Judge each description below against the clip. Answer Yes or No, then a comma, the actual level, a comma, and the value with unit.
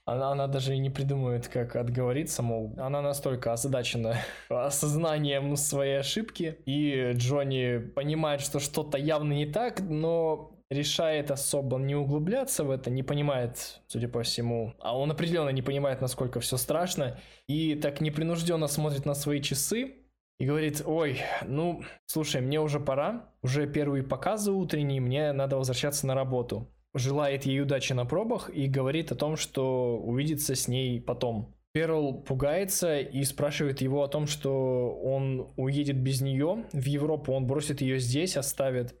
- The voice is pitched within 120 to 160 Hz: Yes, medium, 140 Hz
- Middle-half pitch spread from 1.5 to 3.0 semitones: Yes, narrow, 2.4 semitones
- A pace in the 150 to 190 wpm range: Yes, average, 155 wpm